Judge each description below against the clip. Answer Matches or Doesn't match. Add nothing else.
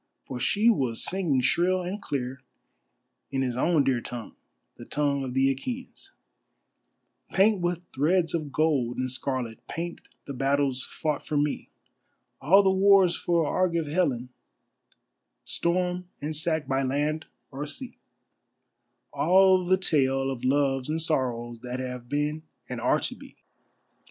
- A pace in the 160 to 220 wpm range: Doesn't match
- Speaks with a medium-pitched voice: Matches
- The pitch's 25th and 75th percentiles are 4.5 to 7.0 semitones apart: Matches